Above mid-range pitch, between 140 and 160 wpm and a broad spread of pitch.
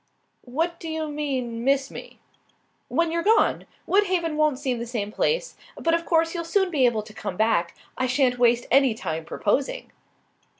No: very high, 275 Hz; average, 175 wpm; wide, 5.8 semitones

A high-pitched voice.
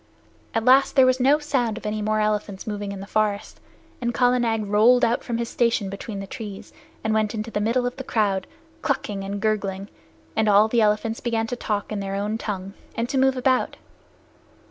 Yes: high, 220 Hz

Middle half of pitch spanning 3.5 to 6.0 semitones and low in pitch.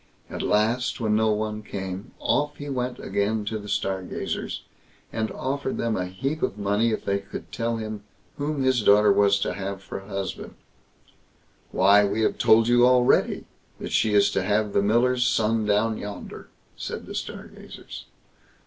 No: average, 2.7 semitones; low, 110 Hz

